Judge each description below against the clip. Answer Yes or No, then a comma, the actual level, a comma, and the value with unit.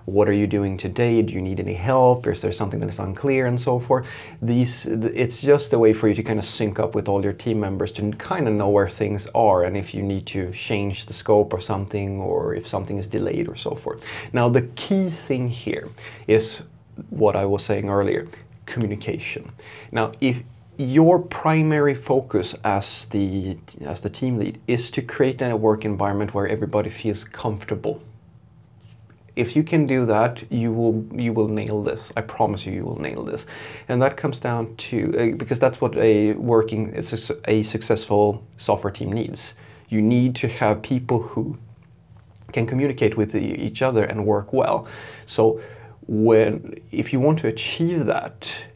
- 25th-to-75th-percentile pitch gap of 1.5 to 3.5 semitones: Yes, average, 2.9 semitones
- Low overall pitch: Yes, low, 110 Hz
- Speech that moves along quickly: No, average, 185 wpm